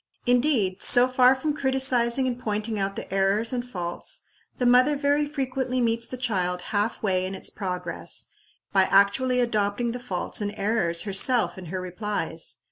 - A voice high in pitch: Yes, high, 225 Hz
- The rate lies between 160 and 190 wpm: Yes, average, 165 wpm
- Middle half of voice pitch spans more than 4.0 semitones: Yes, average, 4.7 semitones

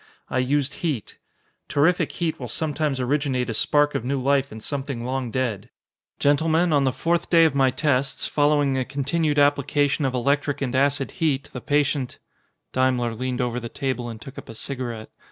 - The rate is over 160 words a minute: Yes, average, 185 wpm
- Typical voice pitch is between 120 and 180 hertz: Yes, low, 135 Hz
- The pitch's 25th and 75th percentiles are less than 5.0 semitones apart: Yes, narrow, 2.4 semitones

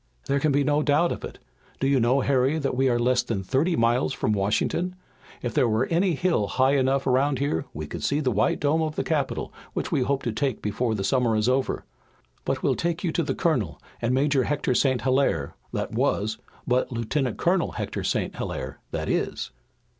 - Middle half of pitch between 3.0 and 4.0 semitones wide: Yes, average, 3.6 semitones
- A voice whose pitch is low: Yes, low, 130 Hz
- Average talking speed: No, fast, 210 wpm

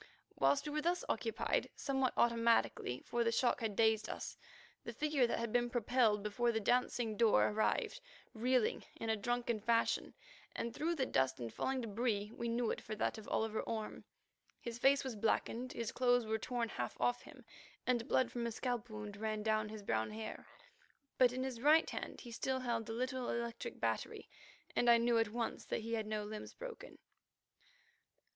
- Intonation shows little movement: Yes, narrow, 2.3 semitones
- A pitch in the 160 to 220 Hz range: No, high, 235 Hz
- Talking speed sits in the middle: Yes, average, 190 wpm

